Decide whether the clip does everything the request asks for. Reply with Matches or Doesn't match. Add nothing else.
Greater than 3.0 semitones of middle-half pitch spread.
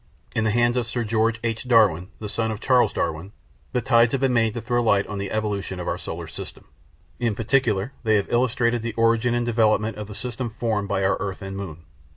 Doesn't match